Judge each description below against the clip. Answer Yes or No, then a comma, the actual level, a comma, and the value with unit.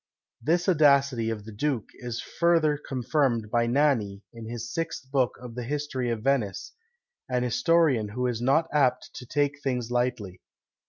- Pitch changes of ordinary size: Yes, average, 3.9 semitones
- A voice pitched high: No, low, 125 Hz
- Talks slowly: No, average, 160 wpm